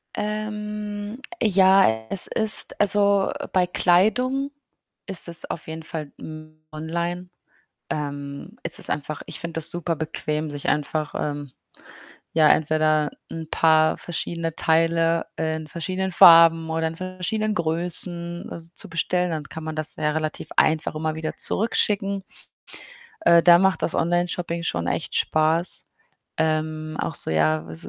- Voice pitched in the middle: Yes, medium, 165 Hz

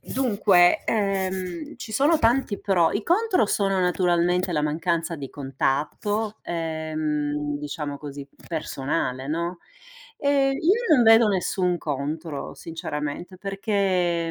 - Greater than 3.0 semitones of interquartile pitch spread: Yes, average, 5.1 semitones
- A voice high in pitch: No, medium, 175 Hz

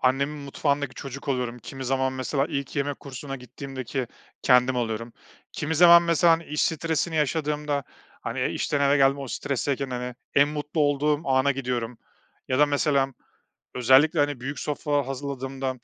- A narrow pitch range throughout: Yes, narrow, 2.1 semitones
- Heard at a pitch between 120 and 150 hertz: Yes, medium, 140 Hz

